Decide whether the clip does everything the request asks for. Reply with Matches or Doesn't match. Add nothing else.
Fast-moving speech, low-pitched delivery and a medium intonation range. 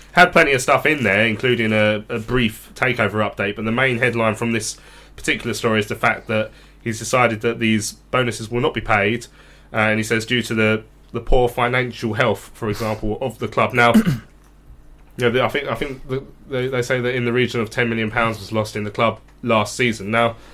Doesn't match